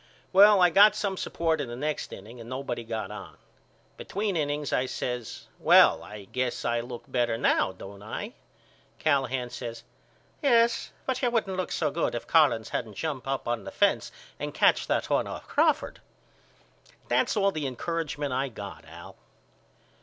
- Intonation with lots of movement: Yes, wide, 6.1 semitones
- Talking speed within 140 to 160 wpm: No, average, 170 wpm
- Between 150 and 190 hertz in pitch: No, low, 135 Hz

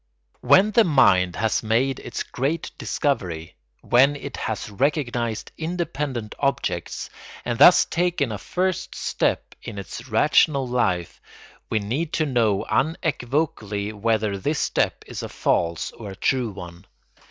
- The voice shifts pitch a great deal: Yes, wide, 6.2 semitones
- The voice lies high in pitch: No, low, 120 Hz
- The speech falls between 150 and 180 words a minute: No, slow, 135 wpm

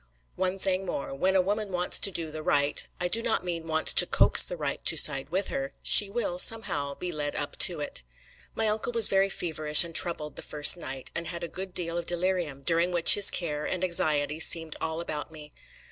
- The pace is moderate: No, fast, 220 wpm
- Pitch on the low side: No, medium, 170 Hz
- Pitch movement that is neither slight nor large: Yes, average, 3.6 semitones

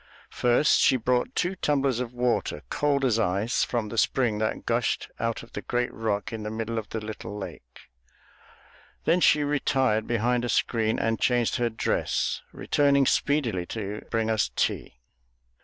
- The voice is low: Yes, low, 115 Hz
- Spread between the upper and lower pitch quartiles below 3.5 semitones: Yes, average, 3.0 semitones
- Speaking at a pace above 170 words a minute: No, average, 165 wpm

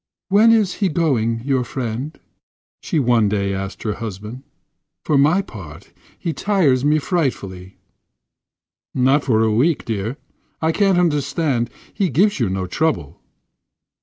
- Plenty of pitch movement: Yes, wide, 6.8 semitones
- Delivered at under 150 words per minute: Yes, slow, 135 wpm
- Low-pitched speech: Yes, low, 130 Hz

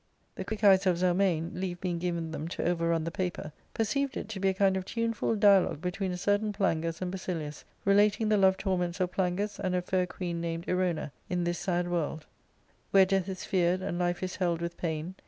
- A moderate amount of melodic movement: No, narrow, 2.1 semitones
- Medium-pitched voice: Yes, medium, 180 Hz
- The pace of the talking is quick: Yes, fast, 225 wpm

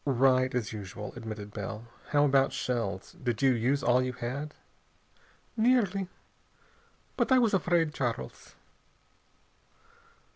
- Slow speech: Yes, slow, 115 wpm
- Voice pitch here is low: Yes, low, 130 Hz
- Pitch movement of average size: Yes, average, 4.8 semitones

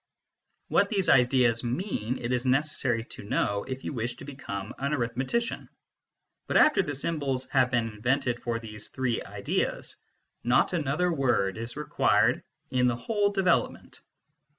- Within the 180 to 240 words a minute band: No, average, 145 wpm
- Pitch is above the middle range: No, low, 130 Hz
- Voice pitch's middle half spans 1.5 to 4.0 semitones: Yes, average, 3.7 semitones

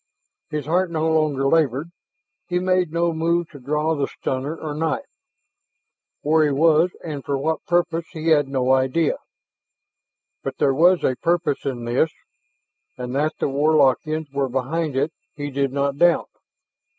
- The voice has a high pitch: No, medium, 155 Hz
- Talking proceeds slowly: No, average, 155 wpm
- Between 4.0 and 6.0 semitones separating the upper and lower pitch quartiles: No, average, 3.1 semitones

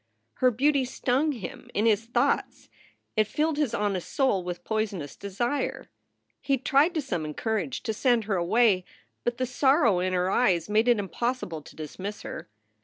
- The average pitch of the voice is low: No, high, 220 Hz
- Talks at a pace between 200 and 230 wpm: No, average, 170 wpm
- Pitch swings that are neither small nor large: No, wide, 5.7 semitones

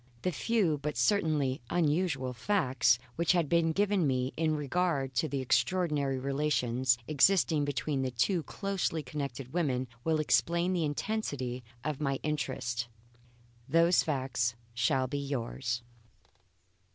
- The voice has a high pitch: No, medium, 145 Hz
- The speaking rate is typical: No, slow, 130 wpm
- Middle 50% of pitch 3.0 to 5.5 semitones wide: Yes, average, 4.3 semitones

